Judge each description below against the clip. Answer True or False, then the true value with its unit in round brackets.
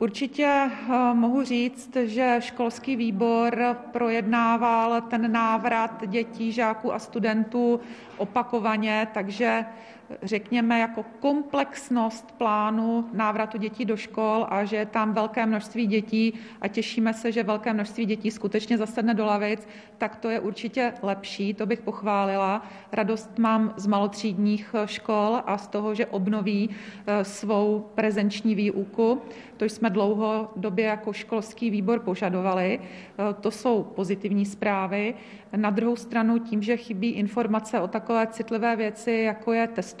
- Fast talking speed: False (130 wpm)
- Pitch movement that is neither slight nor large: False (1.8 semitones)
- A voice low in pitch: False (220 Hz)